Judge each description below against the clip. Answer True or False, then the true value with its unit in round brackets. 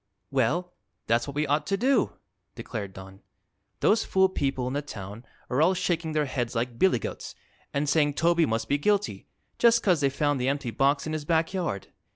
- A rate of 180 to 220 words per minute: True (195 wpm)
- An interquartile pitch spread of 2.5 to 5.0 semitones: False (5.4 semitones)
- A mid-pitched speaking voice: True (145 Hz)